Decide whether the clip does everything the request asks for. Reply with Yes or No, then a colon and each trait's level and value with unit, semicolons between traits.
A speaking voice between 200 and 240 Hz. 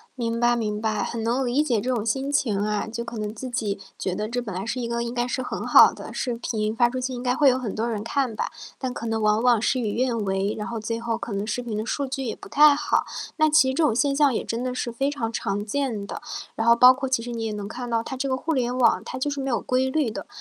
Yes: high, 235 Hz